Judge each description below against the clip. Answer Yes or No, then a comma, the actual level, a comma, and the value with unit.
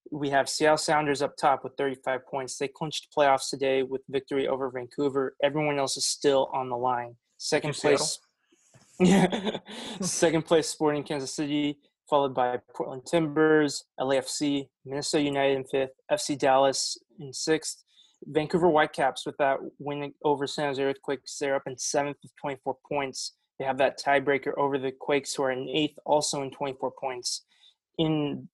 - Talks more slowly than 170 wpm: Yes, average, 160 wpm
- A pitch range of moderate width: No, narrow, 2.1 semitones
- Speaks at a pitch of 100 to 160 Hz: Yes, medium, 140 Hz